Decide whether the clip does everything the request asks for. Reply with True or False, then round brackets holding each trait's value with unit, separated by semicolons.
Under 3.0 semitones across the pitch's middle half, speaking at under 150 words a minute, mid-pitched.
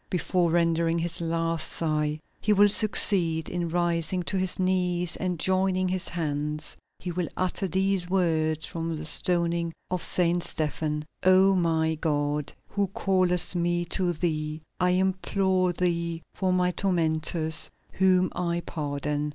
True (2.4 semitones; 140 wpm; 175 Hz)